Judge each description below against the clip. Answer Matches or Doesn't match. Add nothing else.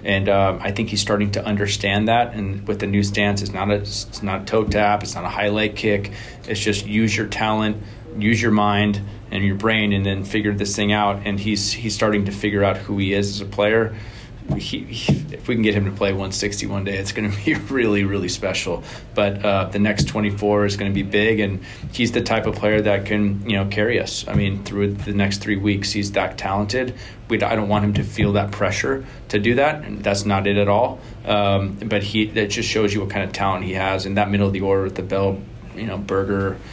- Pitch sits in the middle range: Doesn't match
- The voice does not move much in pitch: Matches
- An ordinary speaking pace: Doesn't match